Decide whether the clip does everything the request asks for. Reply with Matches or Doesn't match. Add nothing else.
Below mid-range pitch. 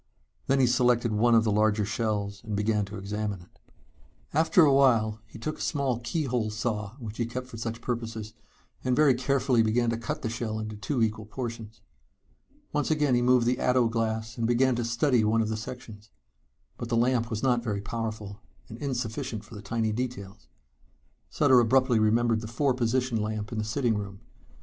Matches